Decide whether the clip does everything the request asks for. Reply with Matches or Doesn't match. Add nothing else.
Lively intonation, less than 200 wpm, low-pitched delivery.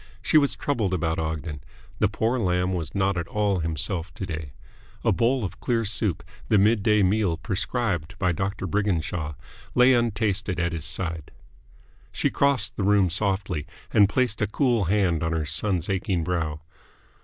Doesn't match